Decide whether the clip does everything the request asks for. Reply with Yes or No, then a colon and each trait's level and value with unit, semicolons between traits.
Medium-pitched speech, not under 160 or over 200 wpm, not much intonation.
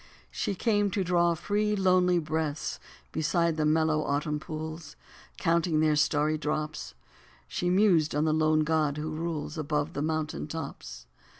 No: medium, 155 Hz; average, 145 wpm; narrow, 2.1 semitones